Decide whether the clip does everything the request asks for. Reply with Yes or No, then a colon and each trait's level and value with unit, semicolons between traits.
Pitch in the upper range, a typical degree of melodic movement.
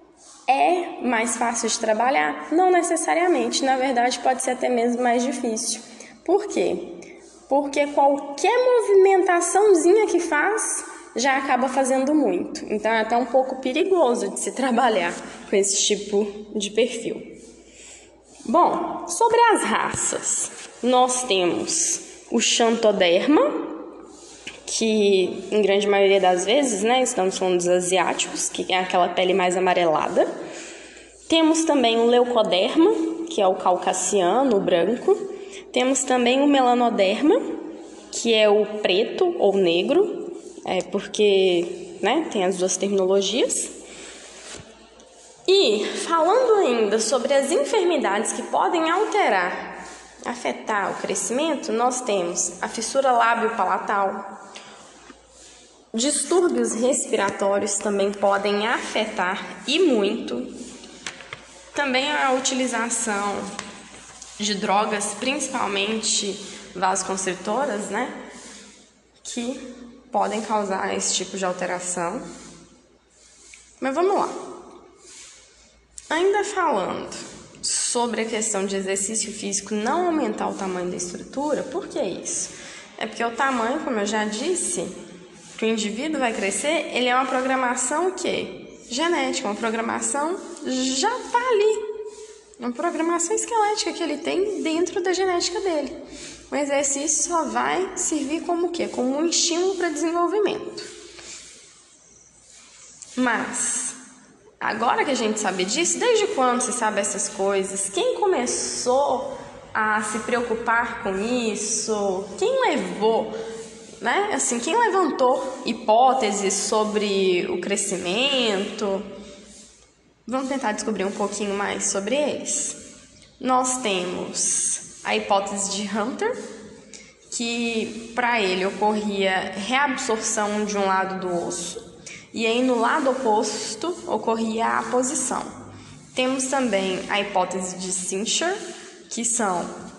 No: high, 245 Hz; wide, 8.4 semitones